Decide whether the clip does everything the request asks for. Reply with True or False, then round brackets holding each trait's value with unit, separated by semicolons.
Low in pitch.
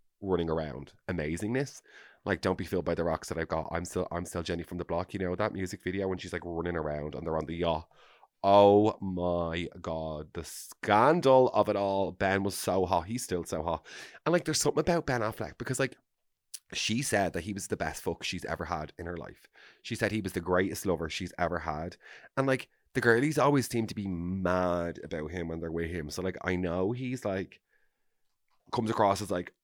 True (95 Hz)